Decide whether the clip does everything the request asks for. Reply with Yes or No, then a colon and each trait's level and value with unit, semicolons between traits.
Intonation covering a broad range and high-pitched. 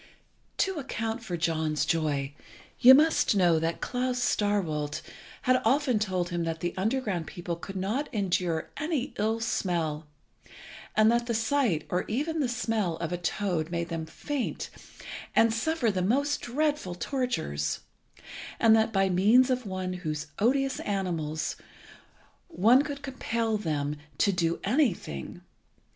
Yes: wide, 6.6 semitones; high, 205 Hz